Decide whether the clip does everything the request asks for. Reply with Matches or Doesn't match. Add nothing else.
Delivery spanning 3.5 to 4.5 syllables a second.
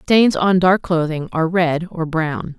Matches